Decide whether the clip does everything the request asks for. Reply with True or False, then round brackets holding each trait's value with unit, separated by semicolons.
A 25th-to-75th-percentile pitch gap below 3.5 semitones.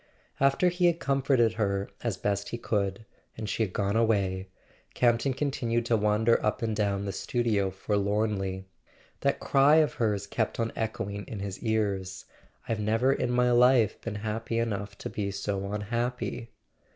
True (2.8 semitones)